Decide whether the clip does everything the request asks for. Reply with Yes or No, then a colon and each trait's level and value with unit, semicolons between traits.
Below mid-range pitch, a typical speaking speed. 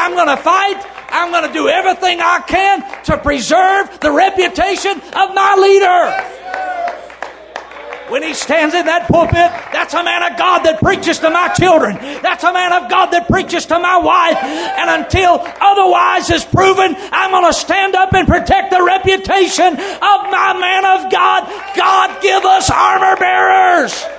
No: very high, 365 Hz; average, 160 wpm